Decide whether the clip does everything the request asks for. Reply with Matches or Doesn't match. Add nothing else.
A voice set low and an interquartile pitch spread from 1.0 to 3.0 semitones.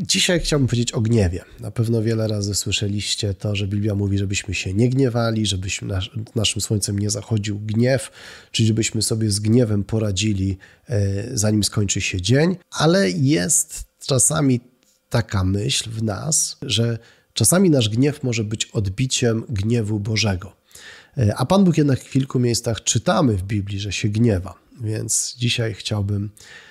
Doesn't match